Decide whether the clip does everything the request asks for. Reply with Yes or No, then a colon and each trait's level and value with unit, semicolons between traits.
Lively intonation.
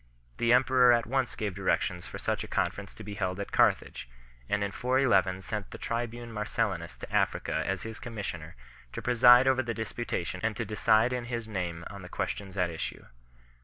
No: average, 3.7 semitones